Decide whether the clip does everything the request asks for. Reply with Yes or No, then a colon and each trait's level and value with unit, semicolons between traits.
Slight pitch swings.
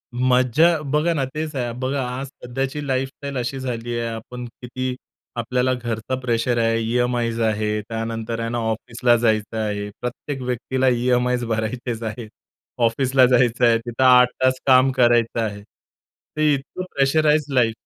Yes: narrow, 2.3 semitones